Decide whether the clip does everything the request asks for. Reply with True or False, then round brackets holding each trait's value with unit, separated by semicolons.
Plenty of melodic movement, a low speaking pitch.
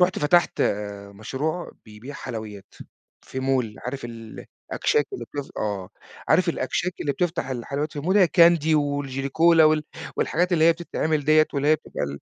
False (5.9 semitones; 145 Hz)